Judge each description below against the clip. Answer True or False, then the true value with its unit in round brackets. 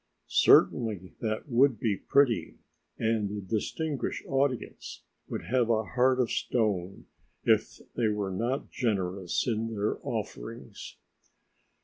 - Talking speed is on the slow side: True (115 wpm)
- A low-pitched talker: True (110 Hz)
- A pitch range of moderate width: True (3.6 semitones)